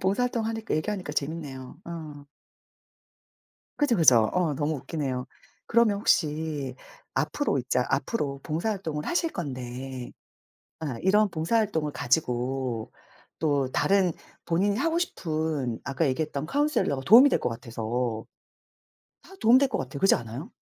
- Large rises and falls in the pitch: Yes, wide, 7.3 semitones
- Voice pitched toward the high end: No, medium, 155 Hz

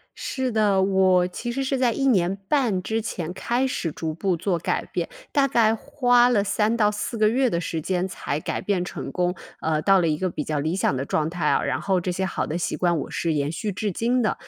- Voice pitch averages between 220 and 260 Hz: No, high, 190 Hz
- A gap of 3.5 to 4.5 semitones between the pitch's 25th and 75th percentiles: No, average, 4.9 semitones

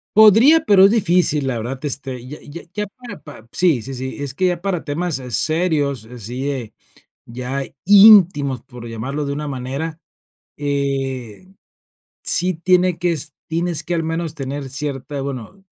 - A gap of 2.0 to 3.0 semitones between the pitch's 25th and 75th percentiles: No, average, 5.0 semitones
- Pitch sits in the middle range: Yes, medium, 145 Hz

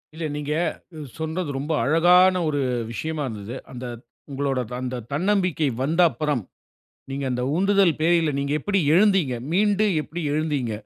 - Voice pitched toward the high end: No, medium, 155 Hz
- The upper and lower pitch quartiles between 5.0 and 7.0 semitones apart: No, average, 4.5 semitones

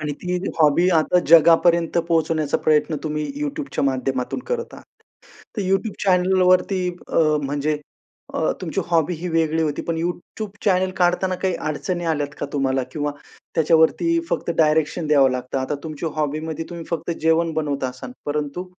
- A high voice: No, medium, 160 Hz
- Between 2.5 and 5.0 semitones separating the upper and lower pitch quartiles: Yes, average, 3.3 semitones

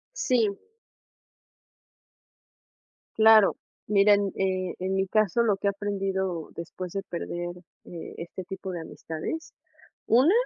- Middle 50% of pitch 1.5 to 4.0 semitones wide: Yes, narrow, 2.4 semitones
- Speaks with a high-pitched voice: Yes, high, 195 Hz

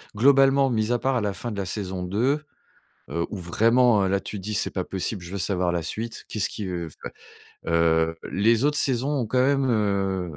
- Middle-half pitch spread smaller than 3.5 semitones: No, average, 4.9 semitones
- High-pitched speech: No, low, 105 Hz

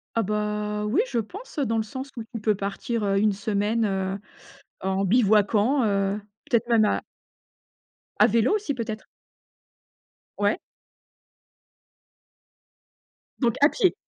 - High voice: Yes, high, 215 Hz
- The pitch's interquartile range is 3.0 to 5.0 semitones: No, narrow, 2.5 semitones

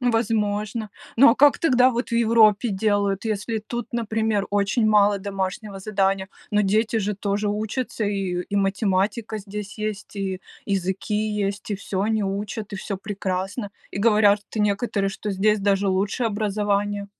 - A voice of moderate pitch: No, high, 205 Hz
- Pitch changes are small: Yes, narrow, 1.8 semitones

